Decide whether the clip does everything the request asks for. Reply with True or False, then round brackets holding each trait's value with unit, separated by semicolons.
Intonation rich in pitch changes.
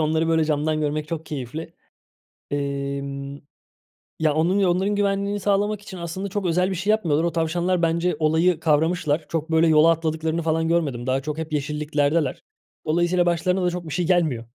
False (2.7 semitones)